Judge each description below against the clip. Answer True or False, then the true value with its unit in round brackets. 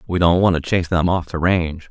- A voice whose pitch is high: False (85 Hz)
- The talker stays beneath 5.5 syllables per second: False (6.3 syllables/s)